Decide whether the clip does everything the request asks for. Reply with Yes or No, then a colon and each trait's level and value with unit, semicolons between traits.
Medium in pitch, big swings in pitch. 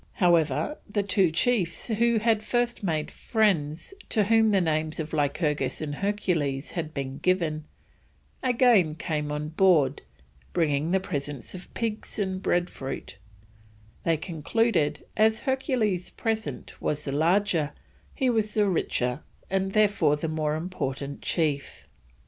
Yes: medium, 175 Hz; wide, 5.9 semitones